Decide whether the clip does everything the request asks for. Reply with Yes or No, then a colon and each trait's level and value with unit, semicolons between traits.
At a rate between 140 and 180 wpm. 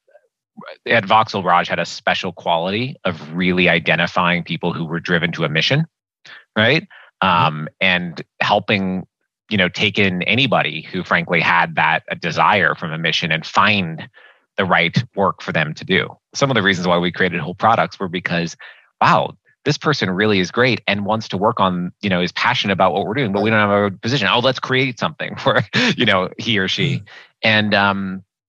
No: average, 195 wpm